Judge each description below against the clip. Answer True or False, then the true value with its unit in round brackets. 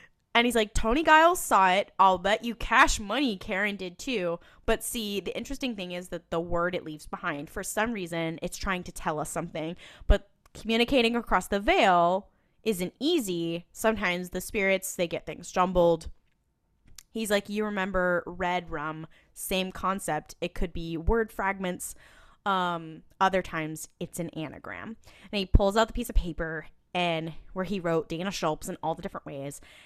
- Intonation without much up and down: False (4.0 semitones)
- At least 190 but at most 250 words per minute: False (175 wpm)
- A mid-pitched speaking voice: True (180 Hz)